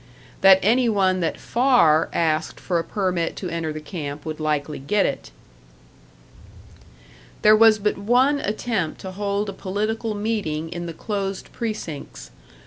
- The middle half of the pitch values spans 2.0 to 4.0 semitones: No, average, 4.8 semitones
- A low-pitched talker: No, high, 195 Hz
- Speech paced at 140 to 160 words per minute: Yes, average, 145 wpm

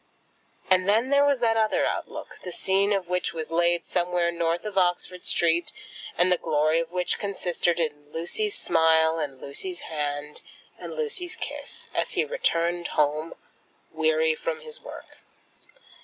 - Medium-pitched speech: Yes, medium, 175 Hz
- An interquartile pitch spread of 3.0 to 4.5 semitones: No, wide, 5.6 semitones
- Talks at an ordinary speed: Yes, average, 155 wpm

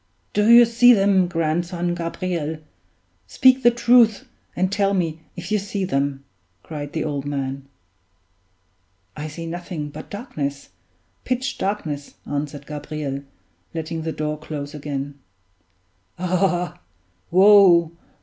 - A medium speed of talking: No, slow, 120 wpm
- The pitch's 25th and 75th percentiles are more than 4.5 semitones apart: Yes, average, 5.0 semitones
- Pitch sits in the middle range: Yes, medium, 170 Hz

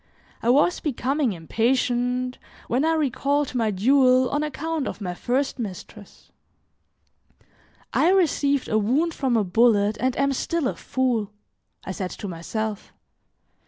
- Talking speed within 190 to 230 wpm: No, slow, 135 wpm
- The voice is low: No, very high, 250 Hz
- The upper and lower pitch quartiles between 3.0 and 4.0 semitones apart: No, average, 4.5 semitones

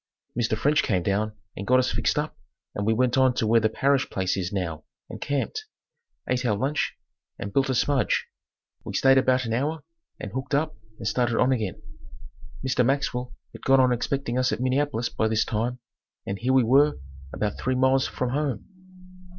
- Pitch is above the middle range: No, low, 125 Hz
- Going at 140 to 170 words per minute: No, average, 190 wpm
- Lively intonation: No, average, 3.6 semitones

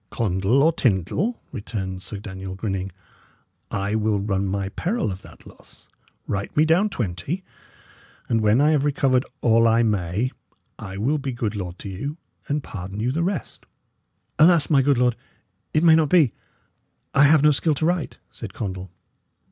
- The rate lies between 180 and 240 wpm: No, average, 170 wpm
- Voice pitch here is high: No, low, 115 Hz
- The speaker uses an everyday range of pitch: No, wide, 7.4 semitones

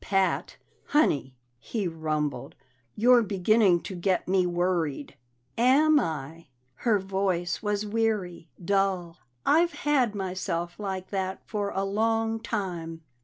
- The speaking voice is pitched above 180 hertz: Yes, high, 190 Hz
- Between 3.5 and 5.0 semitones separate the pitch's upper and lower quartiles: Yes, average, 4.0 semitones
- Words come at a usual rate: No, slow, 120 wpm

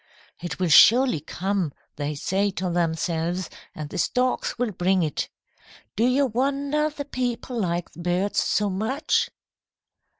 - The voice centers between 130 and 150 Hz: No, high, 195 Hz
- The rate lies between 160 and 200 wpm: No, average, 140 wpm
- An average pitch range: No, wide, 6.4 semitones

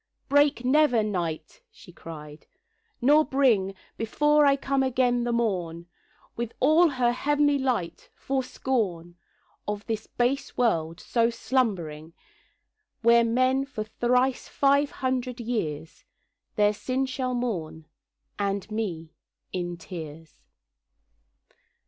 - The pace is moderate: No, slow, 110 wpm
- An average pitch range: No, wide, 6.6 semitones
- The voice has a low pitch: No, high, 235 Hz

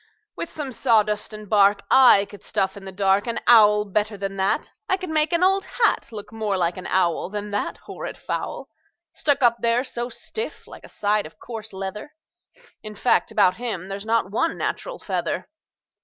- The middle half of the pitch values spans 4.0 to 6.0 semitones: No, average, 3.5 semitones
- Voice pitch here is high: Yes, high, 210 Hz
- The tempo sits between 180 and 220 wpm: Yes, average, 190 wpm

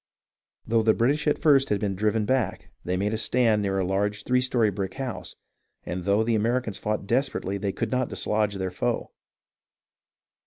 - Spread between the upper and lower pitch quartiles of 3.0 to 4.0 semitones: Yes, average, 3.7 semitones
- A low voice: Yes, low, 110 Hz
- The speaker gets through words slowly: No, average, 185 wpm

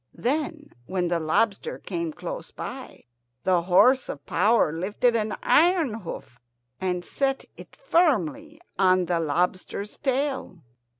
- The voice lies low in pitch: No, high, 210 Hz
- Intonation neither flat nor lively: No, wide, 8.4 semitones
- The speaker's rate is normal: No, slow, 125 wpm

